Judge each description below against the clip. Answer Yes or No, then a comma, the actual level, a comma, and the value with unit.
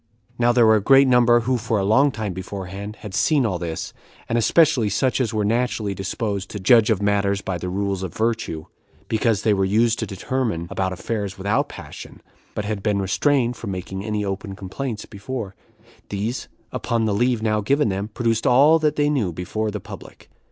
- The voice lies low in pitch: Yes, low, 105 Hz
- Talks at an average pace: Yes, average, 195 wpm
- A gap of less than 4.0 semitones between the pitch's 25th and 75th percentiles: Yes, average, 3.4 semitones